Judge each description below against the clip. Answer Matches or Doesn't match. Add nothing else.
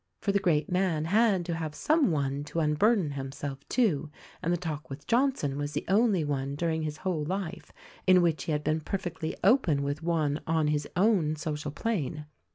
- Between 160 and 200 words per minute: Matches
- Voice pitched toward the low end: Doesn't match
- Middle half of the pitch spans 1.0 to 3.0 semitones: Doesn't match